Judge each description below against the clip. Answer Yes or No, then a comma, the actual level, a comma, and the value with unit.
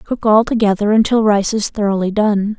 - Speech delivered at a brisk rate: No, average, 185 wpm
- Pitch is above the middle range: Yes, high, 210 Hz